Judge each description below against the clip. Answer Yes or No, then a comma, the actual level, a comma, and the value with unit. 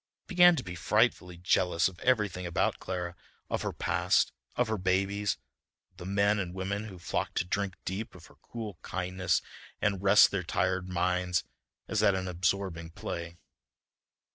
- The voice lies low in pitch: Yes, very low, 95 Hz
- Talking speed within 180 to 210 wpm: No, average, 165 wpm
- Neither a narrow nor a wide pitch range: No, narrow, 2.2 semitones